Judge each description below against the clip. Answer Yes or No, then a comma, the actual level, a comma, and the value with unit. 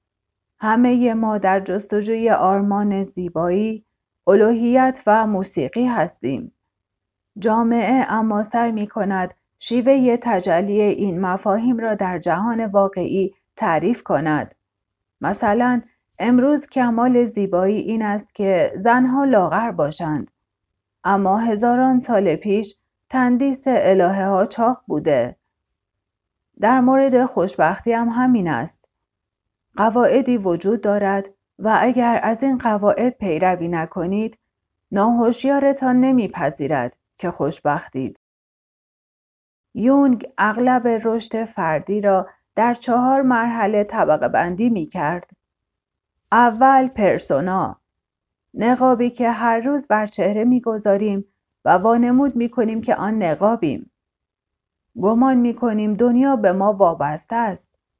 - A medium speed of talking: No, slow, 100 wpm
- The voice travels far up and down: No, average, 4.5 semitones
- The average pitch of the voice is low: No, high, 215 Hz